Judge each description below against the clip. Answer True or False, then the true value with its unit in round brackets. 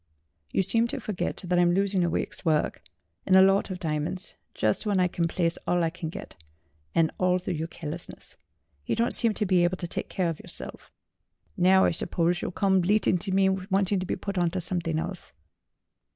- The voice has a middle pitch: True (180 Hz)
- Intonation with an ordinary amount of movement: False (2.2 semitones)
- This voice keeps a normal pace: False (210 wpm)